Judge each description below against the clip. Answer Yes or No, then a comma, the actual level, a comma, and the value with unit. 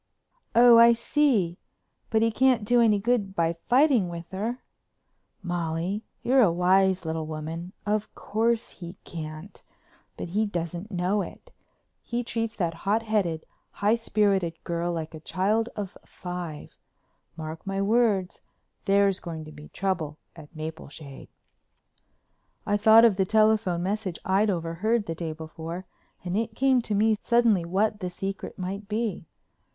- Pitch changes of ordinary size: Yes, average, 4.4 semitones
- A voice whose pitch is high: Yes, high, 195 Hz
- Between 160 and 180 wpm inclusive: No, average, 145 wpm